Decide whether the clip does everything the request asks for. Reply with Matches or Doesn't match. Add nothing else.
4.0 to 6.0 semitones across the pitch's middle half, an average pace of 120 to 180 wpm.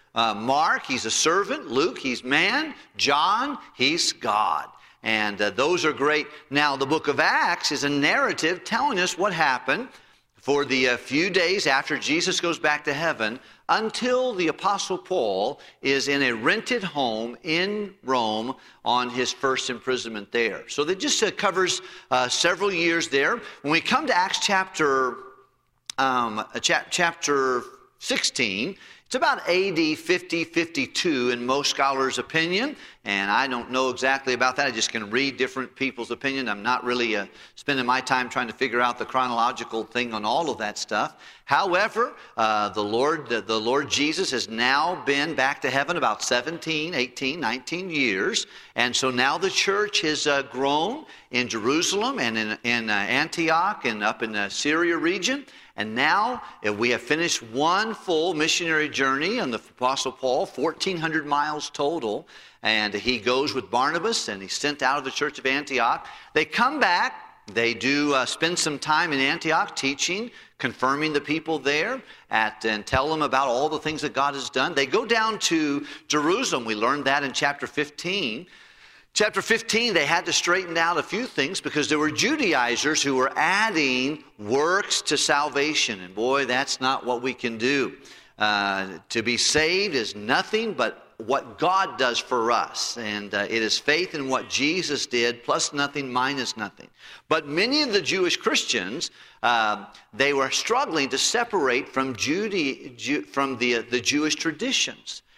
Matches